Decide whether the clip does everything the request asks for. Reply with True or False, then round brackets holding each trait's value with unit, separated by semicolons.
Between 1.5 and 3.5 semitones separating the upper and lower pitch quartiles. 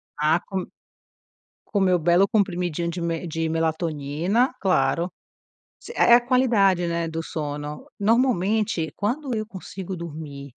False (4.1 semitones)